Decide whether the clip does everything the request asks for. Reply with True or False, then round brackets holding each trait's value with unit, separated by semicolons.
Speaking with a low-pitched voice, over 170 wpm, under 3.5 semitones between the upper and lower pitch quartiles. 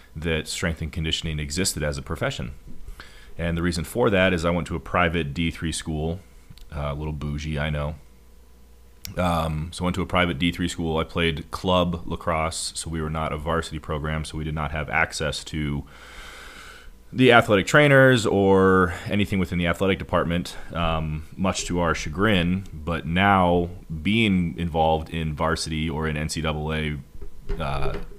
False (80 Hz; 165 wpm; 2.4 semitones)